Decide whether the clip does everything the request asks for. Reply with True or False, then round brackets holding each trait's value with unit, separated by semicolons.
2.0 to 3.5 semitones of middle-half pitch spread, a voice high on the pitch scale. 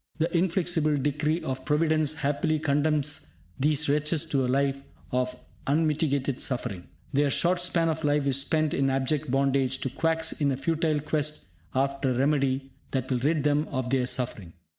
False (2.6 semitones; 145 Hz)